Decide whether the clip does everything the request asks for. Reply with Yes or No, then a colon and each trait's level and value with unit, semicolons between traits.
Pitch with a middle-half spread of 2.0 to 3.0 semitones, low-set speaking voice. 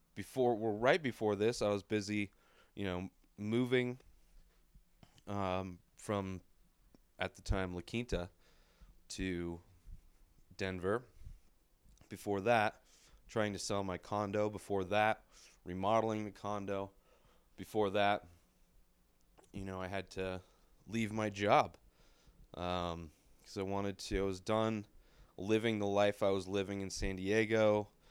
Yes: narrow, 2.6 semitones; low, 100 Hz